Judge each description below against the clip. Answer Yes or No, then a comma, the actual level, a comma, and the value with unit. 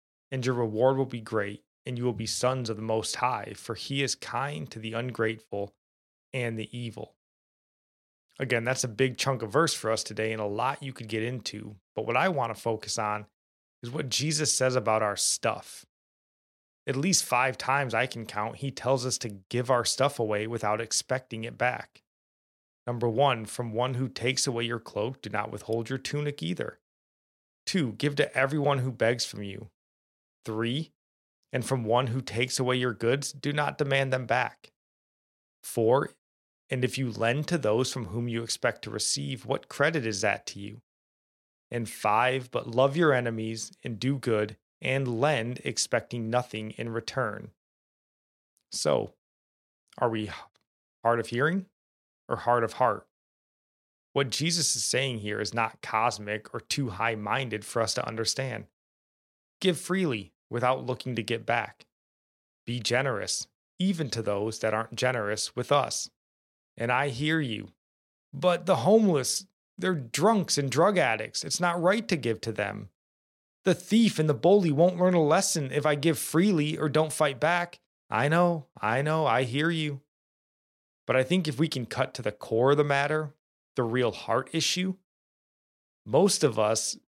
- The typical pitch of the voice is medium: No, low, 125 Hz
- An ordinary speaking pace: Yes, average, 175 wpm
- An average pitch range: Yes, average, 4.7 semitones